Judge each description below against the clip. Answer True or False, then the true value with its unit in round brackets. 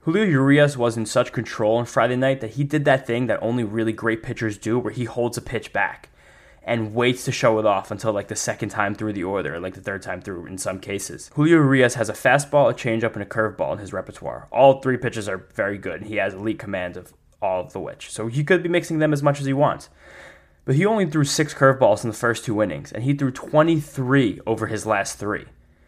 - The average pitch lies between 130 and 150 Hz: False (120 Hz)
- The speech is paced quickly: True (250 wpm)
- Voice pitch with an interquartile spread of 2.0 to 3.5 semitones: False (4.1 semitones)